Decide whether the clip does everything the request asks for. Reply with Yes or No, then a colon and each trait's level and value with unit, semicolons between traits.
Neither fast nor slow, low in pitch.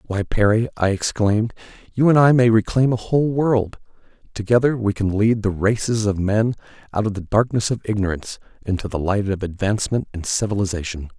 Yes: average, 175 wpm; low, 105 Hz